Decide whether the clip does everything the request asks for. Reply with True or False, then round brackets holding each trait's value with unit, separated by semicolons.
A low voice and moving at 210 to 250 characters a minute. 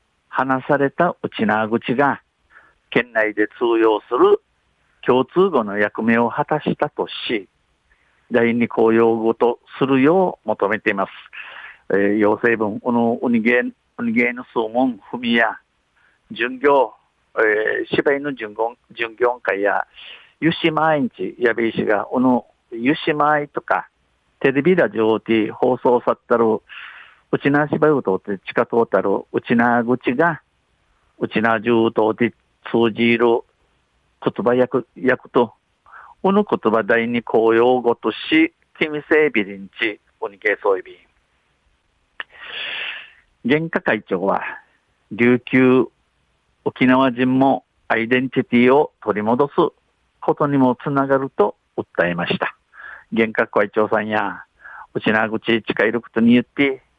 True (120 Hz; 235 characters per minute)